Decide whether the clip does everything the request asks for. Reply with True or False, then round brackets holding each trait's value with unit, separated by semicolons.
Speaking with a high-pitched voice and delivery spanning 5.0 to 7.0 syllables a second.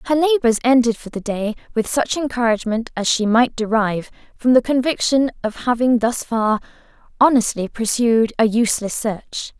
True (235 Hz; 5.1 syllables/s)